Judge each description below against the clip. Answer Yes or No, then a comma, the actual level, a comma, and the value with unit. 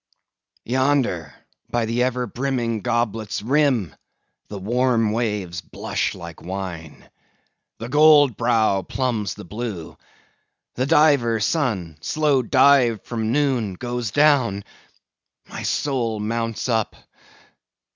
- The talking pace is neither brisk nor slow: No, slow, 95 wpm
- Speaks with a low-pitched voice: Yes, low, 115 Hz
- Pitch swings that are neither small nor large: Yes, average, 3.9 semitones